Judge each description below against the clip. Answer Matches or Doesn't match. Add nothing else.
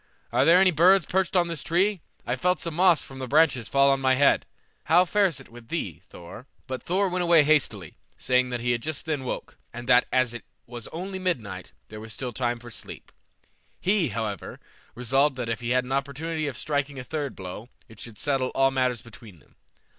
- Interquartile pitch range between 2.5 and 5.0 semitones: Doesn't match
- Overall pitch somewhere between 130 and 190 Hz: Matches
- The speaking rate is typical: Doesn't match